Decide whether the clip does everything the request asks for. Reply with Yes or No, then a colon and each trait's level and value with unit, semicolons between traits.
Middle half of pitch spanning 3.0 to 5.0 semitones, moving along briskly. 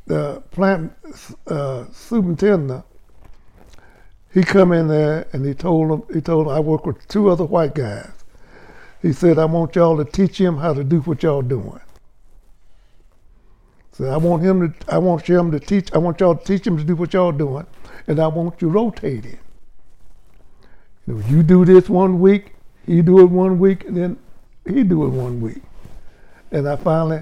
No: average, 4.6 semitones; average, 185 wpm